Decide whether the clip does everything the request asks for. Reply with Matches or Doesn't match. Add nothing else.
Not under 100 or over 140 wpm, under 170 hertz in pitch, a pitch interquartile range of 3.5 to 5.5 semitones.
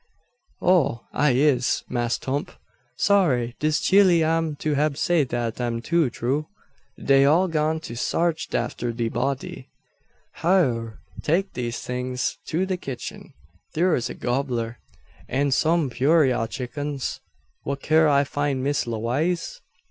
Matches